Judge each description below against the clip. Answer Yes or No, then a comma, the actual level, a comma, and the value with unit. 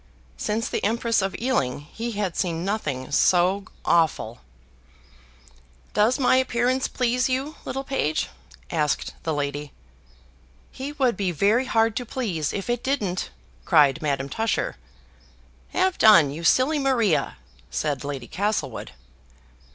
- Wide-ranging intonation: Yes, wide, 8.3 semitones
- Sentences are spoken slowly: Yes, slow, 130 wpm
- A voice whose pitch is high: Yes, high, 205 Hz